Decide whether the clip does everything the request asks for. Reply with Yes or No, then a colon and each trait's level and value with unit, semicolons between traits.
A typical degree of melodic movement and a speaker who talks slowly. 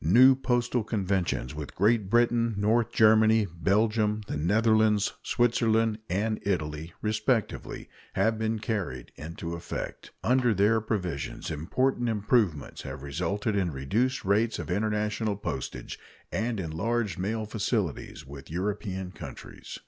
Yes: average, 3.7 semitones; slow, 120 wpm